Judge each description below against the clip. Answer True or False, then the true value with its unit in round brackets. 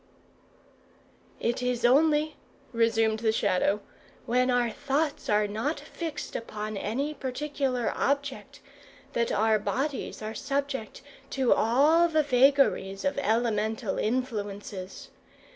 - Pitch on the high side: True (245 Hz)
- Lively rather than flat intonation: False (4.5 semitones)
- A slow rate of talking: True (110 wpm)